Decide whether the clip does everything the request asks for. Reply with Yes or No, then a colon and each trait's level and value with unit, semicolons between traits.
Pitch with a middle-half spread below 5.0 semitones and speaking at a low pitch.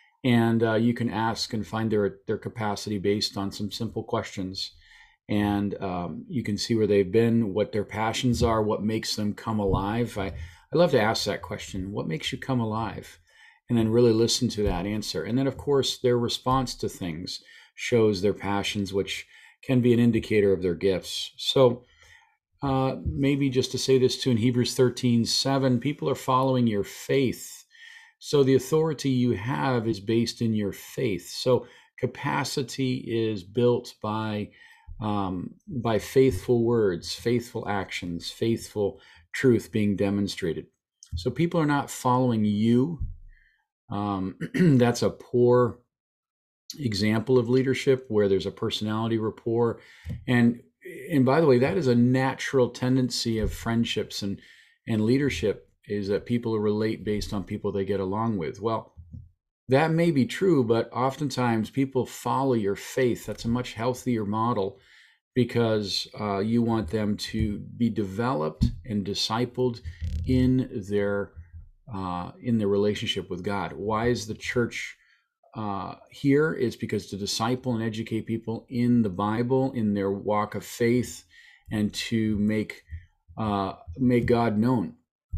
Yes: average, 3.4 semitones; low, 115 Hz